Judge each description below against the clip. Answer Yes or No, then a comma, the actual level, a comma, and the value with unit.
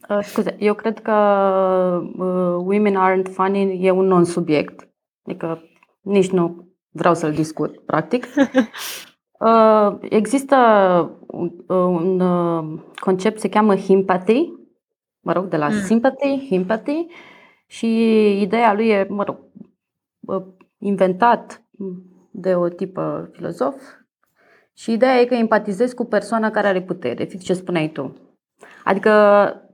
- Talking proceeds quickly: No, average, 125 wpm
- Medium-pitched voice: No, high, 195 Hz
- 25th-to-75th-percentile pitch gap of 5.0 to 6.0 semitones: No, average, 3.4 semitones